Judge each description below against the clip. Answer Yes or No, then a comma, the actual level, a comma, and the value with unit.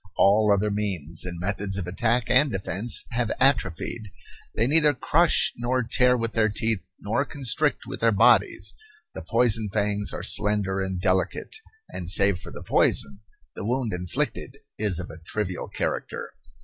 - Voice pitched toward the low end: Yes, low, 105 Hz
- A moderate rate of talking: Yes, average, 160 wpm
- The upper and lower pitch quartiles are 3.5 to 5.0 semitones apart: Yes, average, 3.9 semitones